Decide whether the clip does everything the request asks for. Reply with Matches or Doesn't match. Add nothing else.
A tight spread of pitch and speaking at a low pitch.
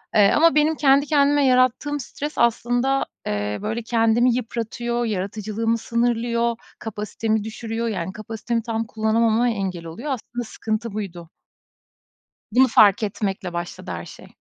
Doesn't match